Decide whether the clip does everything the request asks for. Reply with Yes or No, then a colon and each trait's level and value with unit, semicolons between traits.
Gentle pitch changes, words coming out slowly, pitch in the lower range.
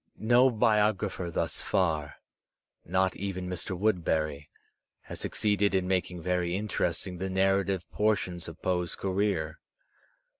Yes: narrow, 2.3 semitones; slow, 120 wpm; very low, 95 Hz